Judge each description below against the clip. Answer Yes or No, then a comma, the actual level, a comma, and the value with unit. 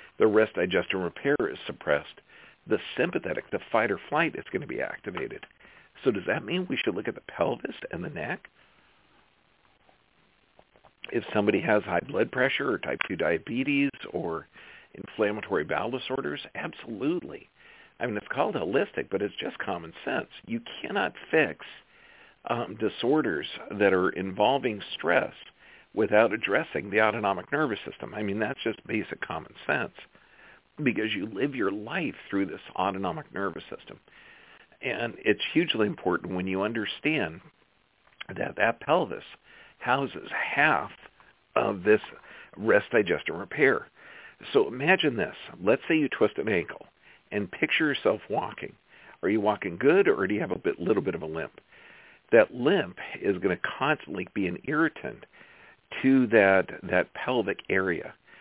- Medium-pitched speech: No, very high, 395 Hz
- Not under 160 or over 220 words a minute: No, average, 150 wpm